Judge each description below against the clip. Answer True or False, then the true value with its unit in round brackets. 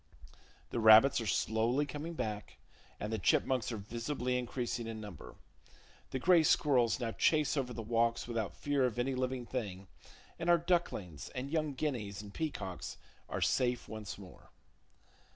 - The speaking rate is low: False (155 wpm)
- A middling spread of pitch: True (4.0 semitones)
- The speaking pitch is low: True (120 Hz)